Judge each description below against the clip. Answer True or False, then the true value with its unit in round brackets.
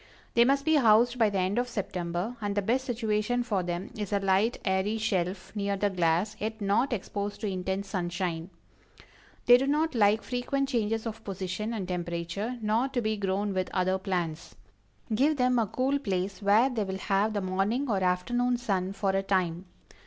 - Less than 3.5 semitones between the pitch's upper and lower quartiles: False (4.0 semitones)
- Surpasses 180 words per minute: True (190 wpm)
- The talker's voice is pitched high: True (205 Hz)